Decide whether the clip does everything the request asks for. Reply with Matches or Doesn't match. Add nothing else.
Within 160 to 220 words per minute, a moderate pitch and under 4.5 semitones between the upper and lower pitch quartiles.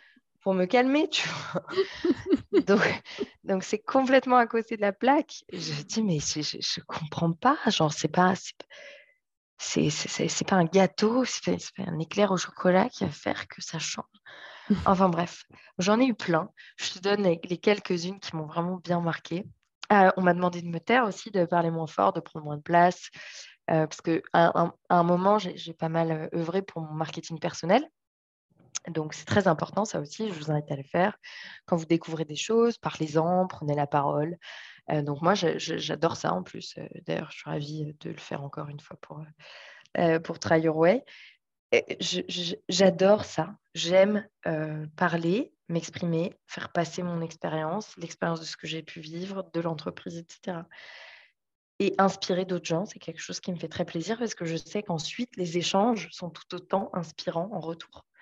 Matches